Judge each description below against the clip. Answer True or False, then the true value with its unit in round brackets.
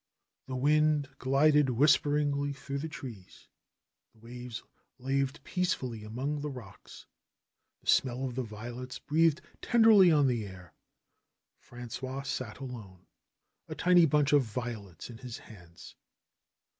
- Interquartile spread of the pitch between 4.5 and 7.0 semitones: False (3.9 semitones)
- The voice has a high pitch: False (130 Hz)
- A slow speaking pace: True (125 wpm)